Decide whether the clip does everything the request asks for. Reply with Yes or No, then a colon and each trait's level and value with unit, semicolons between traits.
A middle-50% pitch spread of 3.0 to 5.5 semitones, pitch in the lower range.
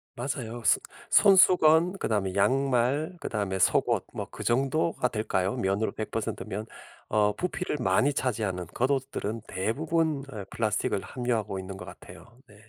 Yes: average, 5.2 semitones; low, 120 Hz